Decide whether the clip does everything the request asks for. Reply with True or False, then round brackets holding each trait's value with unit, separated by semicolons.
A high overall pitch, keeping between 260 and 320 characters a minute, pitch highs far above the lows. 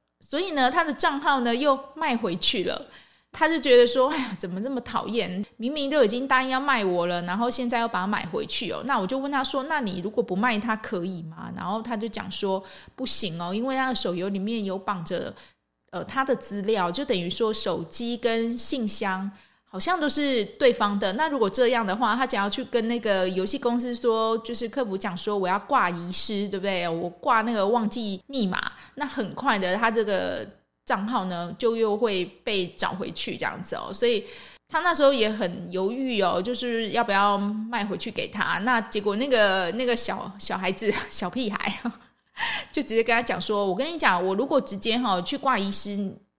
False (225 Hz; 290 characters per minute; 4.4 semitones)